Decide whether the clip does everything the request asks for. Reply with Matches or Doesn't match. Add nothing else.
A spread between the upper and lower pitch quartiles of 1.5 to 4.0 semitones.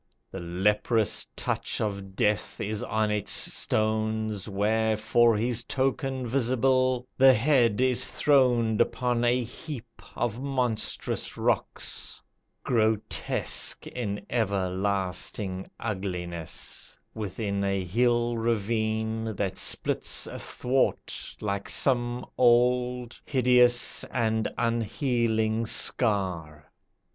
Matches